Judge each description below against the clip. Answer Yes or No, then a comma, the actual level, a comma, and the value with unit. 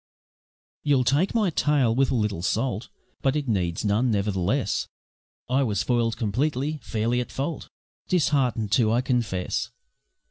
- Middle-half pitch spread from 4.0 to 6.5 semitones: Yes, average, 4.6 semitones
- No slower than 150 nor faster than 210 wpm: No, average, 140 wpm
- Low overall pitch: Yes, low, 120 Hz